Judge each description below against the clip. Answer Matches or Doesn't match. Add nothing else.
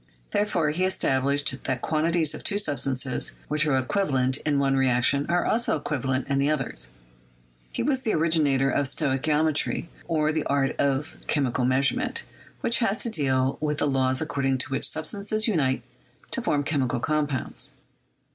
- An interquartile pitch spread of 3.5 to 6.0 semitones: Doesn't match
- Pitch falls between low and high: Matches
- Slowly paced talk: Doesn't match